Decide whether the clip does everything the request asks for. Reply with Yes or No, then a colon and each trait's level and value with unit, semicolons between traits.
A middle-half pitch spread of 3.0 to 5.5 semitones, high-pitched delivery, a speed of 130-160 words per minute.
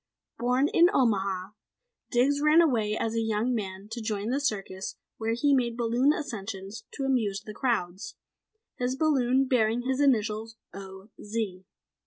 Yes: average, 4.1 semitones; high, 230 Hz; average, 150 wpm